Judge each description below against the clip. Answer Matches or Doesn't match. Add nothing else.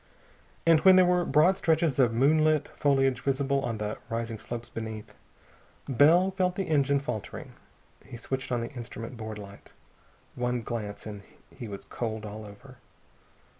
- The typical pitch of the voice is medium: Doesn't match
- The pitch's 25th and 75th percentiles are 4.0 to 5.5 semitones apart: Matches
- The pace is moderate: Matches